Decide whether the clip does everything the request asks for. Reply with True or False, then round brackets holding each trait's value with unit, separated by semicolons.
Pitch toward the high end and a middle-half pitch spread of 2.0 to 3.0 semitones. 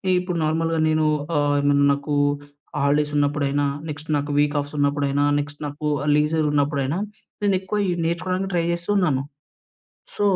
False (150 Hz; 2.6 semitones)